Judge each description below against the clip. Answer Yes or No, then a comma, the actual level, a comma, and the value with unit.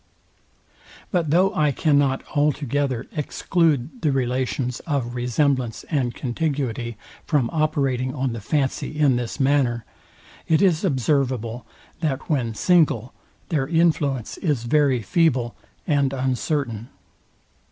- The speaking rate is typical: No, slow, 110 wpm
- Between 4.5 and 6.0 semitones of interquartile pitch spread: No, average, 3.7 semitones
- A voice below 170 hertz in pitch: Yes, low, 135 Hz